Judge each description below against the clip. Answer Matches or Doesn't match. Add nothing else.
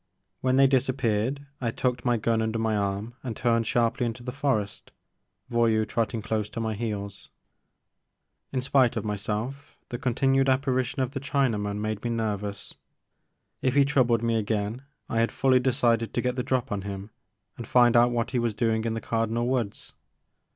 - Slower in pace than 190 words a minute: Matches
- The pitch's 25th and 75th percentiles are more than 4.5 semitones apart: Doesn't match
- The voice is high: Doesn't match